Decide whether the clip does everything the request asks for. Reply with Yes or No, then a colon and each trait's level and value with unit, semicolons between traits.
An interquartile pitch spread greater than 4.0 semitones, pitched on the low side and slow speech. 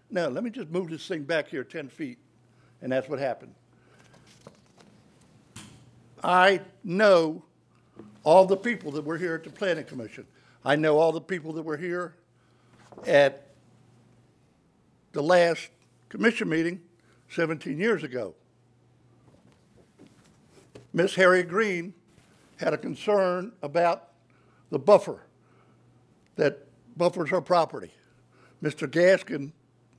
No: average, 5.0 semitones; medium, 165 Hz; slow, 115 wpm